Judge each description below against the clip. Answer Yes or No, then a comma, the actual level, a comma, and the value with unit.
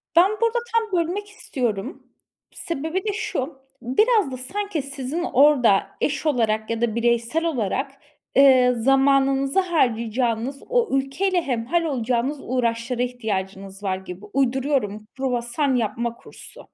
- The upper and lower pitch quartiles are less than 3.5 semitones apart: No, average, 5.2 semitones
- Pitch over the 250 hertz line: Yes, very high, 265 Hz